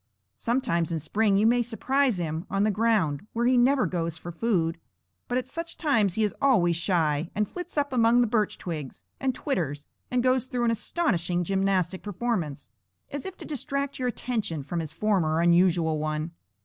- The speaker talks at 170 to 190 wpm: Yes, average, 185 wpm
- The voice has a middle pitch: No, high, 205 Hz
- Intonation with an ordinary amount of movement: No, wide, 6.6 semitones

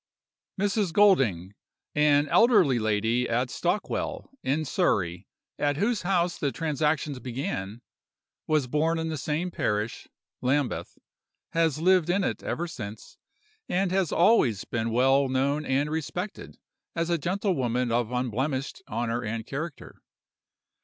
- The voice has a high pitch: No, medium, 145 Hz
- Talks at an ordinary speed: No, slow, 125 wpm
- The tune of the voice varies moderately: No, wide, 5.9 semitones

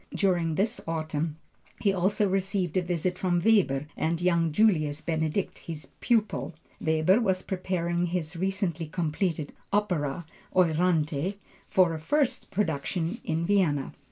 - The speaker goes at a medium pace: No, slow, 130 wpm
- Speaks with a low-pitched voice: No, medium, 175 Hz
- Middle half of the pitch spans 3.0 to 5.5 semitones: Yes, average, 3.4 semitones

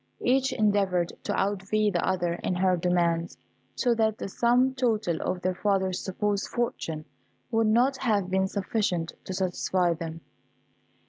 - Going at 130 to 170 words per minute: Yes, average, 145 wpm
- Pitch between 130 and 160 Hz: No, high, 190 Hz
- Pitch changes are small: No, average, 3.5 semitones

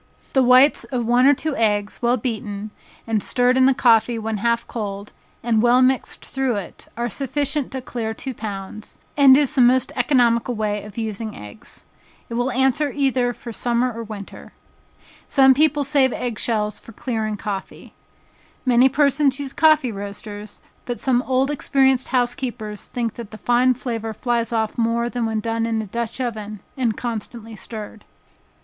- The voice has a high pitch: Yes, high, 235 Hz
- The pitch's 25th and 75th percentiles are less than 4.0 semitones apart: Yes, average, 3.1 semitones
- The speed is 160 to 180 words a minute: Yes, average, 170 wpm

